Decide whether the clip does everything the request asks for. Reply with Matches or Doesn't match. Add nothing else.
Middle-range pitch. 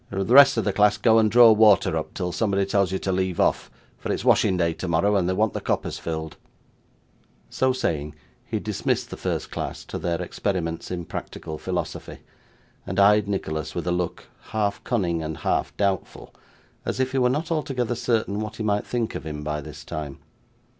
Doesn't match